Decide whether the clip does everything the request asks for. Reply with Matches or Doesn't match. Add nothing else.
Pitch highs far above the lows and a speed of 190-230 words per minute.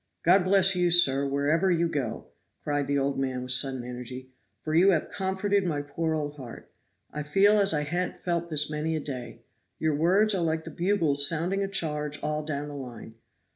Doesn't match